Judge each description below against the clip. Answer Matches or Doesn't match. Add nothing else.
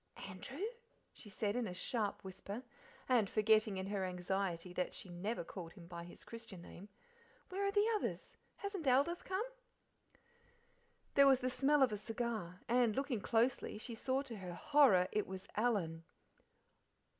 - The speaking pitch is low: Doesn't match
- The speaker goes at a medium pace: Matches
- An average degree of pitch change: Doesn't match